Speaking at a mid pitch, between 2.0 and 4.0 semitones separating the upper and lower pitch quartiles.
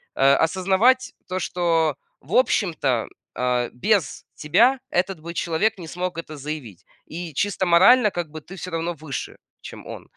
Yes: medium, 170 Hz; average, 3.6 semitones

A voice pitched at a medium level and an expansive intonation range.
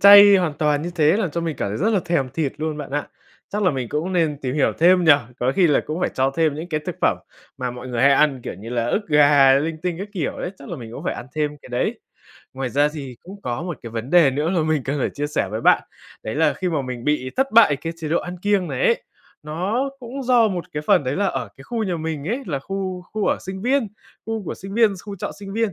Yes: medium, 160 Hz; wide, 5.7 semitones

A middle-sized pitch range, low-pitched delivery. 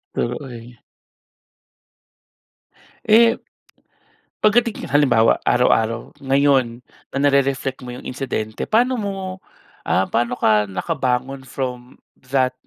Yes: average, 3.1 semitones; low, 130 Hz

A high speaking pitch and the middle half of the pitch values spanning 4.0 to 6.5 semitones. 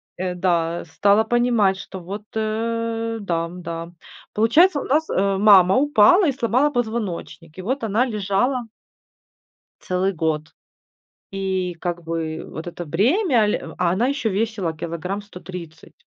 Yes: high, 200 Hz; average, 4.7 semitones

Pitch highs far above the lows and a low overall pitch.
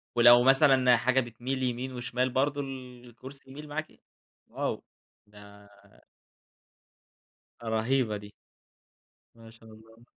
No: average, 2.8 semitones; low, 125 Hz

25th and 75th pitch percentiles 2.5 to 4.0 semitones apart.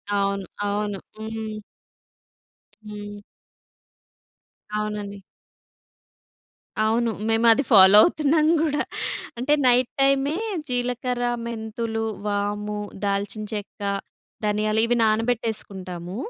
Yes: average, 2.8 semitones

